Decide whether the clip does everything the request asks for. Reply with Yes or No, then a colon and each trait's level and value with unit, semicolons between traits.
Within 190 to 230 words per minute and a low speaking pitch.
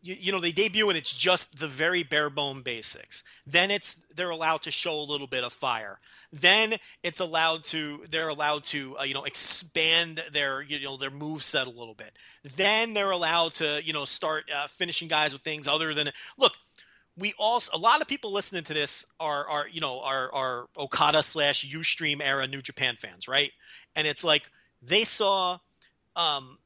No: average, 195 wpm; medium, 155 Hz